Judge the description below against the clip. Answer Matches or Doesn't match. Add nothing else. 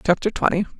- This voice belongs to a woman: Matches